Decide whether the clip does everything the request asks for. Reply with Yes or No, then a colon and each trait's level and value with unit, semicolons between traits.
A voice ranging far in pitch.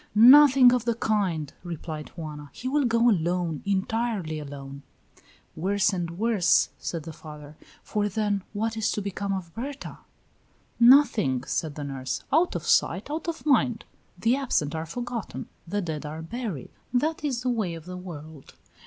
Yes: wide, 6.9 semitones